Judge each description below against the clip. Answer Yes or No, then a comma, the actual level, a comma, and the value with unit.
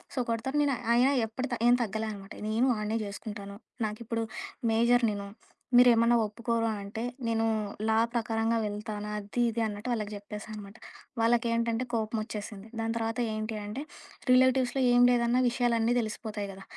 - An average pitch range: No, narrow, 2.0 semitones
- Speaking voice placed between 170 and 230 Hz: Yes, high, 225 Hz